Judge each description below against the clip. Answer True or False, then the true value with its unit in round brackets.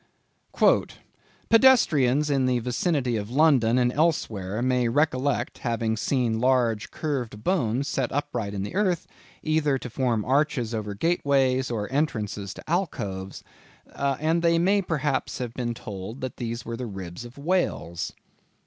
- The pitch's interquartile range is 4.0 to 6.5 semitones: True (4.7 semitones)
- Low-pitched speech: True (130 Hz)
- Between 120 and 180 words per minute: True (145 wpm)